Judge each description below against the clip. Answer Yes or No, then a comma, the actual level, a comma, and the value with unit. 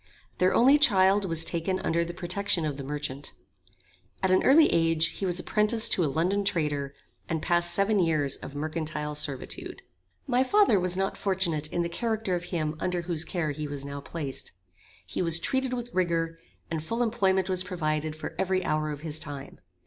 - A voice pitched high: No, medium, 170 Hz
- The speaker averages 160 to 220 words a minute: Yes, average, 185 wpm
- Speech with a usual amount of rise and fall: Yes, average, 3.9 semitones